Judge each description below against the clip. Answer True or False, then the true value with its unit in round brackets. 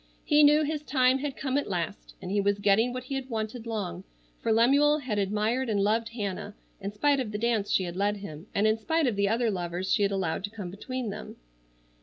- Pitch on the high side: True (215 Hz)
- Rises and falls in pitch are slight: False (4.3 semitones)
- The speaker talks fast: True (235 wpm)